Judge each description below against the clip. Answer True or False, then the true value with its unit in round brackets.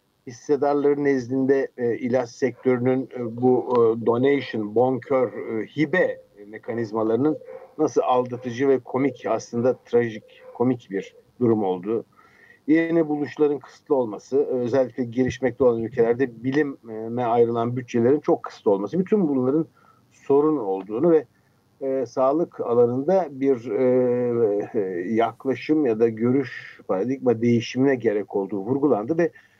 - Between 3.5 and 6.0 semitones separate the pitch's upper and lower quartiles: False (3.1 semitones)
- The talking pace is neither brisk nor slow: True (120 wpm)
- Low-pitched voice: True (130 Hz)